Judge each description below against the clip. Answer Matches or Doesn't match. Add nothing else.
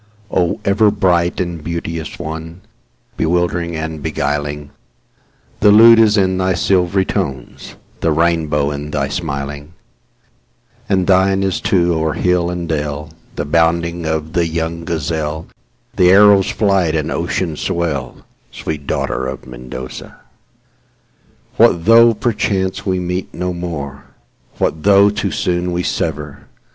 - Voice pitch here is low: Matches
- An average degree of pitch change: Matches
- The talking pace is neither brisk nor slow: Doesn't match